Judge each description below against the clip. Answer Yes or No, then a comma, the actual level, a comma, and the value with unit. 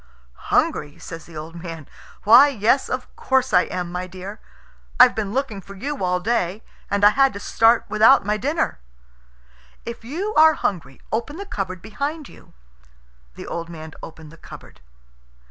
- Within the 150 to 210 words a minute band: Yes, average, 165 wpm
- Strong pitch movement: Yes, wide, 6.7 semitones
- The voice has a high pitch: Yes, high, 210 Hz